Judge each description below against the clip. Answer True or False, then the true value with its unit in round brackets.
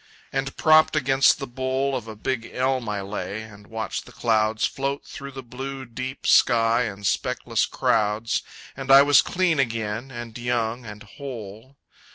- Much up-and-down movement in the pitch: False (3.6 semitones)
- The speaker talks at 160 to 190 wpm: True (165 wpm)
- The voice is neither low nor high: False (120 Hz)